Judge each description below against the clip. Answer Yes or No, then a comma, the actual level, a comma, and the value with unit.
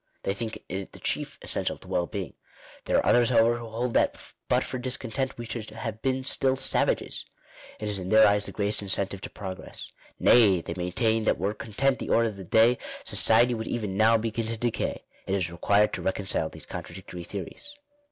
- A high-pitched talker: No, low, 110 Hz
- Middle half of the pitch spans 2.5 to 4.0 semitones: Yes, average, 3.2 semitones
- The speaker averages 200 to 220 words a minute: Yes, fast, 205 wpm